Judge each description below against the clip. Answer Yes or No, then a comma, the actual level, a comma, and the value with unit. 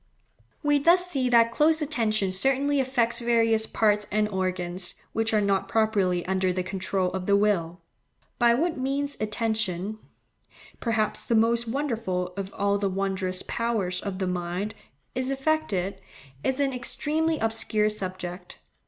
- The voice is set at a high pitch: Yes, high, 215 Hz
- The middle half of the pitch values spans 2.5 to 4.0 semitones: No, average, 4.8 semitones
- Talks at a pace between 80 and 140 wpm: Yes, slow, 135 wpm